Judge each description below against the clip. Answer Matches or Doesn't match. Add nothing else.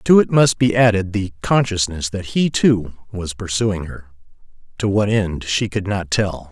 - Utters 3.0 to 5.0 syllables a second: Matches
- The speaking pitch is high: Doesn't match